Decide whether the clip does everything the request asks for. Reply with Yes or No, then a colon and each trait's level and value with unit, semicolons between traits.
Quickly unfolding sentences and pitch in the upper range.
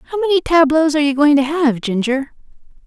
No: average, 190 wpm; very high, 295 Hz